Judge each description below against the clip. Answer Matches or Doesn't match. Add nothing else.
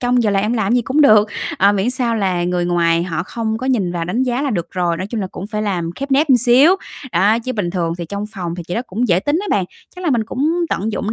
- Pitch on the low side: Doesn't match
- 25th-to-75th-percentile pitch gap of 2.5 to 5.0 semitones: Doesn't match